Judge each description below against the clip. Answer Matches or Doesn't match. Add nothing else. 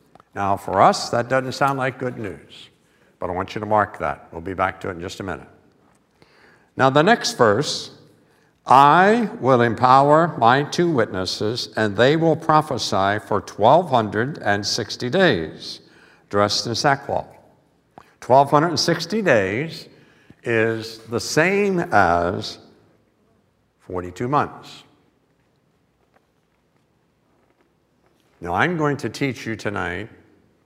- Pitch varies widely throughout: Matches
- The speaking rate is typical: Doesn't match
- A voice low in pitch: Matches